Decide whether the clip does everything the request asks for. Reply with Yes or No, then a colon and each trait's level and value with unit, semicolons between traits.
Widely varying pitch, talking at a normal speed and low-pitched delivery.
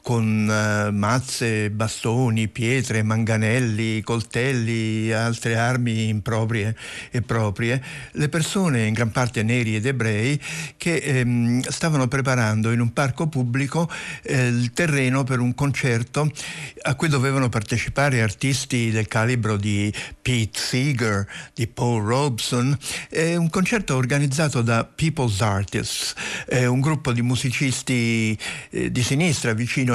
No: average, 3.4 semitones; average, 125 wpm; low, 125 Hz